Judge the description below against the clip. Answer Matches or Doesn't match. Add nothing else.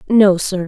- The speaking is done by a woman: Matches